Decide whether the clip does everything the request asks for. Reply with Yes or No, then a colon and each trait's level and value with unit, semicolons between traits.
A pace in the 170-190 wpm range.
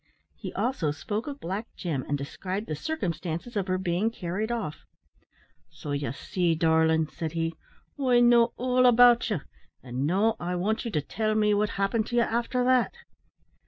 Yes: average, 175 wpm